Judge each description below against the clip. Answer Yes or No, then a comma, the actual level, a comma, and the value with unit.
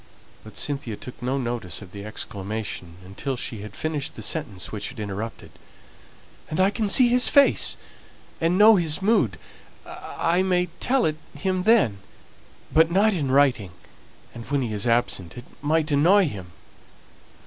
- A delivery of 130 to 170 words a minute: Yes, average, 160 wpm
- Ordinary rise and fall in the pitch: No, wide, 8.7 semitones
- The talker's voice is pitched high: No, medium, 140 Hz